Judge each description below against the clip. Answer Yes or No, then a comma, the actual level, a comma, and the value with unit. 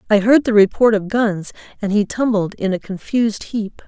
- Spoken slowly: No, average, 200 wpm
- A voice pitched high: Yes, high, 210 Hz